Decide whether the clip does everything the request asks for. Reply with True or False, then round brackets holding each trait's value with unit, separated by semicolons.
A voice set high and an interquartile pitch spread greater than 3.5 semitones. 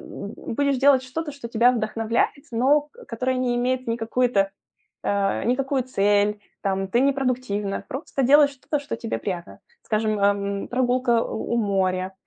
True (240 Hz; 4.3 semitones)